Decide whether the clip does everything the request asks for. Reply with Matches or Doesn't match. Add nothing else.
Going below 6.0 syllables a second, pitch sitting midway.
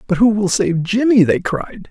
Doesn't match